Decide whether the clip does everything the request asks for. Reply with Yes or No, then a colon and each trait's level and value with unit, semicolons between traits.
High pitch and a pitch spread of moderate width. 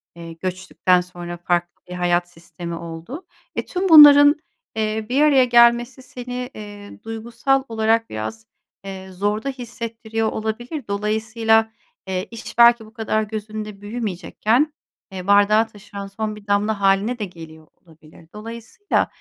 Yes: high, 215 Hz; average, 4.2 semitones